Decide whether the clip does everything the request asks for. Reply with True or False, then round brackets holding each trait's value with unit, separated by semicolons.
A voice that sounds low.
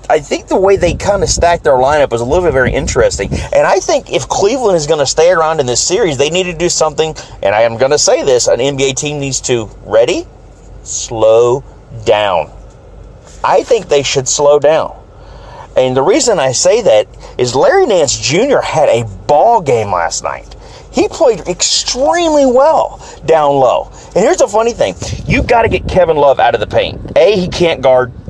False (155 Hz)